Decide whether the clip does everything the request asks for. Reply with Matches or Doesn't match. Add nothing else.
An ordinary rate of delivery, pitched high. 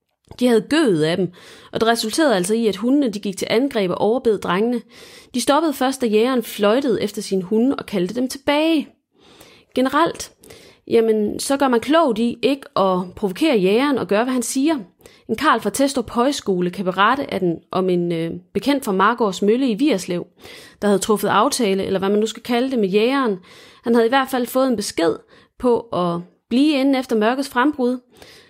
Matches